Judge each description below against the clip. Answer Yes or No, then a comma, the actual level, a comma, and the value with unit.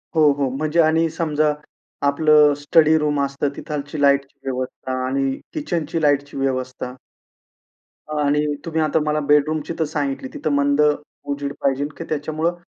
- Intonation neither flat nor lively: No, narrow, 1.8 semitones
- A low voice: No, medium, 145 Hz